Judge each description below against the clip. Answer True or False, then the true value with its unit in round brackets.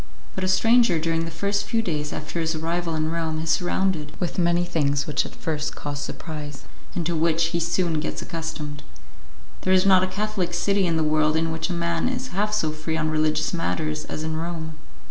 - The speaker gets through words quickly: True (210 wpm)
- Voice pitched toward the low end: False (165 Hz)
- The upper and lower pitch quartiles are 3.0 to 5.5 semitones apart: False (2.4 semitones)